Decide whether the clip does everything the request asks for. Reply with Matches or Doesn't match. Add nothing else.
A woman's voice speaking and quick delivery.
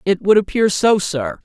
Doesn't match